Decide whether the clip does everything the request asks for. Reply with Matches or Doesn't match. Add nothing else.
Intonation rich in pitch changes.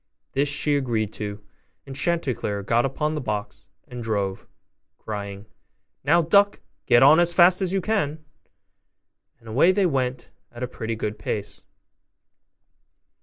Matches